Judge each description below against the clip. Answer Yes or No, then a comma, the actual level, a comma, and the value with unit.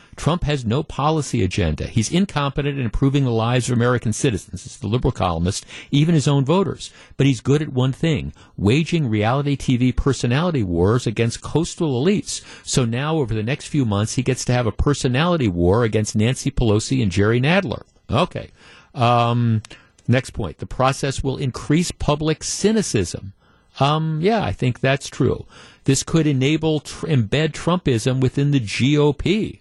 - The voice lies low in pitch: Yes, low, 130 Hz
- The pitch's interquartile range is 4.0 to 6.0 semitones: Yes, average, 4.5 semitones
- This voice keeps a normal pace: Yes, average, 165 wpm